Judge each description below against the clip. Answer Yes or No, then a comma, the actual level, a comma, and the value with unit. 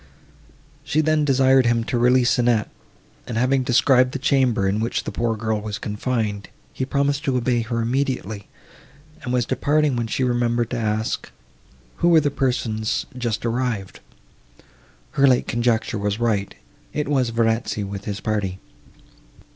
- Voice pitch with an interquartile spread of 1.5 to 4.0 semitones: Yes, average, 3.1 semitones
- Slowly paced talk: No, average, 155 wpm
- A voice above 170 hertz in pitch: No, low, 120 Hz